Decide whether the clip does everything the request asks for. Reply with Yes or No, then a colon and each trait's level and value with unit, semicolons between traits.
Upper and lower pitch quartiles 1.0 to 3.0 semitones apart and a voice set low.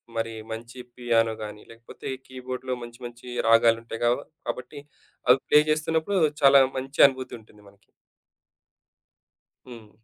Yes: narrow, 2.4 semitones; low, 120 Hz